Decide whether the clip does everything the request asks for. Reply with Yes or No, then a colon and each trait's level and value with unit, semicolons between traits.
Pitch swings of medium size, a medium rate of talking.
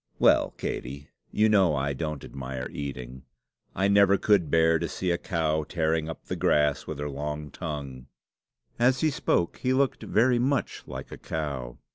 No: wide, 5.8 semitones; average, 170 wpm